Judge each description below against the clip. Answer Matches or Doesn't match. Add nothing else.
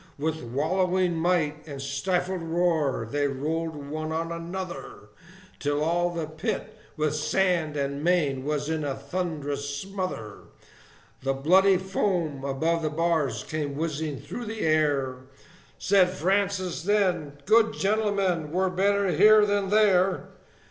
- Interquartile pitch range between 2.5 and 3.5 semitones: Doesn't match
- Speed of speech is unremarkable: Doesn't match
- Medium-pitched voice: Matches